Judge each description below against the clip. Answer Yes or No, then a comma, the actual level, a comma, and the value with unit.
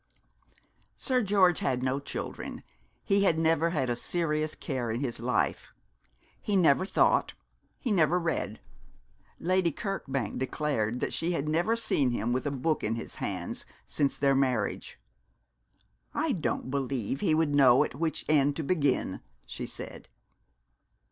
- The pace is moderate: Yes, average, 150 wpm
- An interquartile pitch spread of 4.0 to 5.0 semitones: Yes, average, 4.6 semitones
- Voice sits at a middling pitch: Yes, medium, 145 Hz